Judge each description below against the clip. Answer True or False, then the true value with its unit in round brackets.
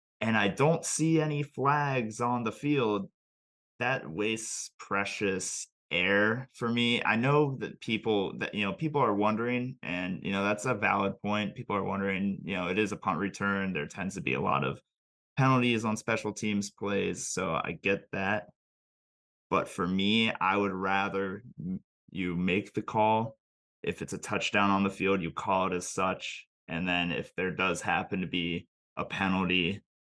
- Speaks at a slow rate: False (180 wpm)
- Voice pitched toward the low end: True (100 Hz)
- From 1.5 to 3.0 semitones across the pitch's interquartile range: False (3.7 semitones)